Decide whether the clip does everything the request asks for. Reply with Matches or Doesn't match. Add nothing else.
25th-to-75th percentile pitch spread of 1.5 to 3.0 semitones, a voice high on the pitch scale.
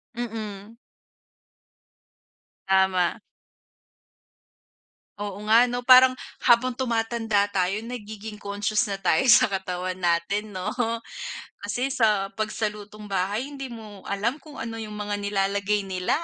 Matches